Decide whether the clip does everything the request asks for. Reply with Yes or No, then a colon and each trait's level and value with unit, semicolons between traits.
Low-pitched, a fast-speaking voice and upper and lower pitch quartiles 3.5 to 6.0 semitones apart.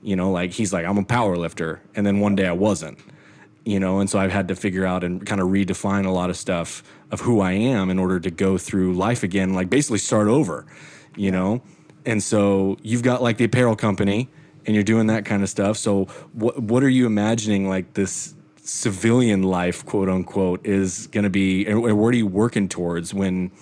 No: low, 100 Hz; fast, 220 wpm; average, 2.7 semitones